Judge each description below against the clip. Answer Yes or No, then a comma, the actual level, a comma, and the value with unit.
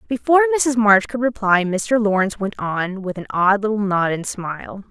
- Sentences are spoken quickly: No, average, 195 wpm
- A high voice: Yes, high, 210 Hz